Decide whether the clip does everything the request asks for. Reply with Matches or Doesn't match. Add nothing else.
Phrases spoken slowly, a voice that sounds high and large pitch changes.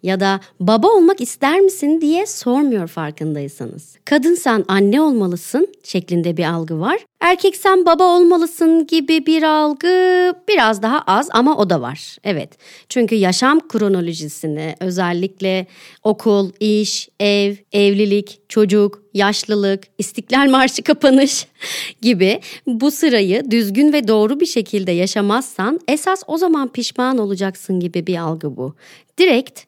Doesn't match